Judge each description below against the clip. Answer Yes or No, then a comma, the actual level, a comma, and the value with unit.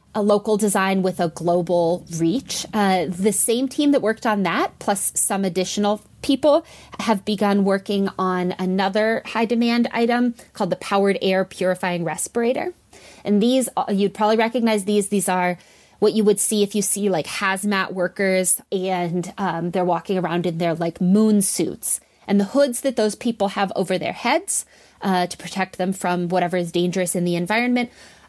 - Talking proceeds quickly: No, average, 170 wpm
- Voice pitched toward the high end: Yes, high, 195 Hz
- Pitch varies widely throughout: No, average, 3.0 semitones